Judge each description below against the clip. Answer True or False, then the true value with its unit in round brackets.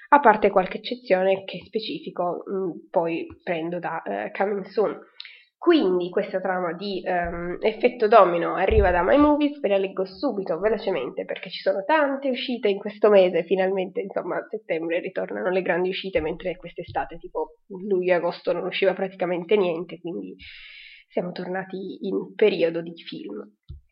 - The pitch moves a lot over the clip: False (3.4 semitones)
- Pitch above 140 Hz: True (190 Hz)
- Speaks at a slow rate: False (155 wpm)